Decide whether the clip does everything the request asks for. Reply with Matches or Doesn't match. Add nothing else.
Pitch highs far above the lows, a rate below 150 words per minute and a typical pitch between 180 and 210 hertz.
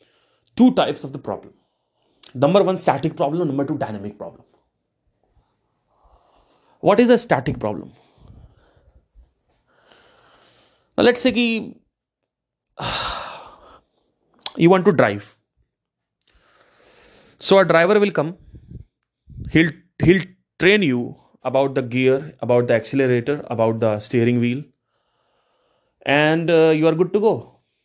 Doesn't match